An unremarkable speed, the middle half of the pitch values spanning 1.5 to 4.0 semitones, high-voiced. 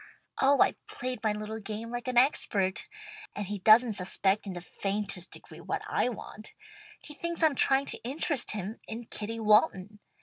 Yes: average, 175 wpm; average, 3.4 semitones; high, 220 Hz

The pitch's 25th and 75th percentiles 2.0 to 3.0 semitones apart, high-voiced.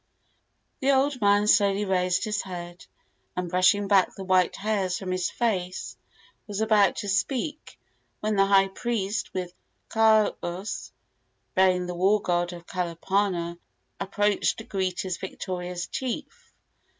Yes: average, 2.7 semitones; high, 195 Hz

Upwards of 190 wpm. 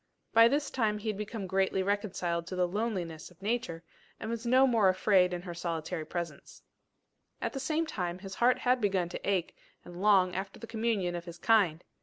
Yes: average, 200 wpm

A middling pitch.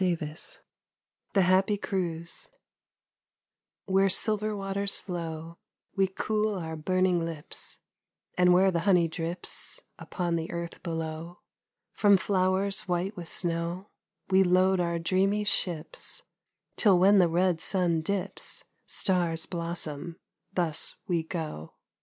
Yes: medium, 180 Hz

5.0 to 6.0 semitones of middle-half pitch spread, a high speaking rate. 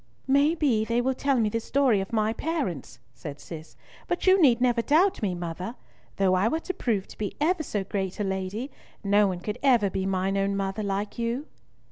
Yes: wide, 5.5 semitones; fast, 210 wpm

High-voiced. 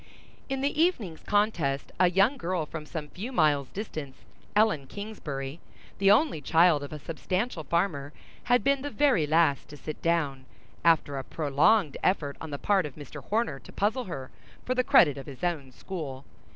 No: medium, 165 Hz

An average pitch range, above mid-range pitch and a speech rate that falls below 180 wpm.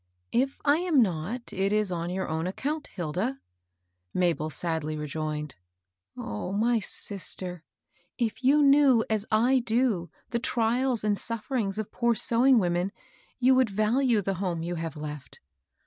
No: wide, 6.3 semitones; high, 210 Hz; average, 165 wpm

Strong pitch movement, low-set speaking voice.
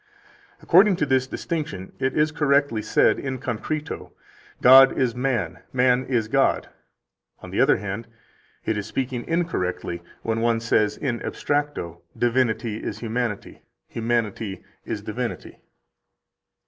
No: average, 3.7 semitones; low, 120 Hz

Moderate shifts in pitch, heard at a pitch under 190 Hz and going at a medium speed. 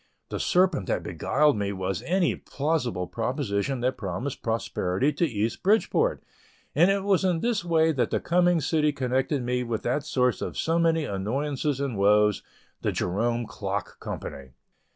No: wide, 7.3 semitones; low, 135 Hz; average, 160 wpm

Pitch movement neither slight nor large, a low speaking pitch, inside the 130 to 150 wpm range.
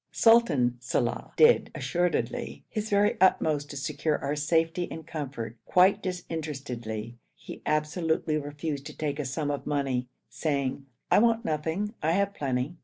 No: average, 4.3 semitones; medium, 150 Hz; average, 145 wpm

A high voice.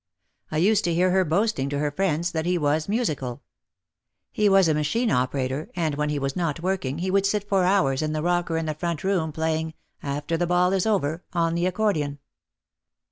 No: medium, 165 Hz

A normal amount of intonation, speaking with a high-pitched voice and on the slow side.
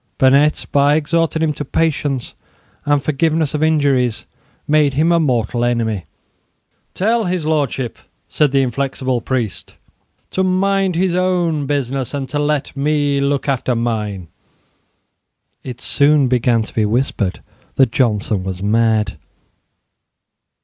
No: average, 4.3 semitones; medium, 140 Hz; slow, 130 wpm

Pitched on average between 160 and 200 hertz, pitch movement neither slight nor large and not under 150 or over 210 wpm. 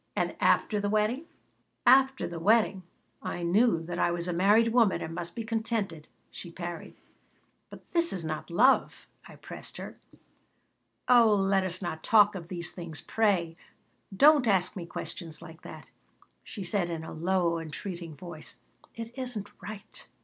Yes: high, 190 Hz; average, 4.7 semitones; average, 160 wpm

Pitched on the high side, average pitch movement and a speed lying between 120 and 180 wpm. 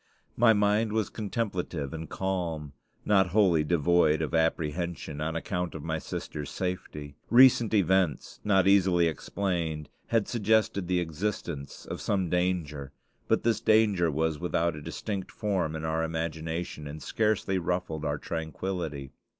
No: very low, 85 Hz; average, 3.8 semitones; average, 140 wpm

